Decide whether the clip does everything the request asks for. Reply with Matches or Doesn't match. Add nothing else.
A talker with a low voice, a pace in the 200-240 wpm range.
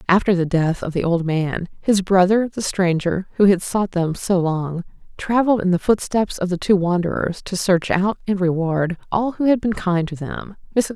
Doesn't match